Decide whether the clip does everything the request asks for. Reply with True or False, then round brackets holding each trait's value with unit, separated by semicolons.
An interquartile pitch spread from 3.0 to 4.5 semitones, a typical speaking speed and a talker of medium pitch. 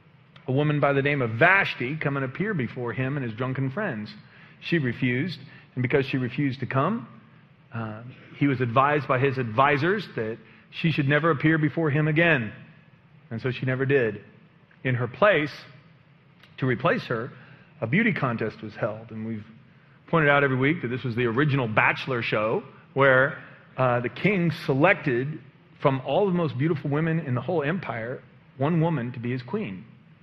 True (3.7 semitones; 175 wpm; 145 Hz)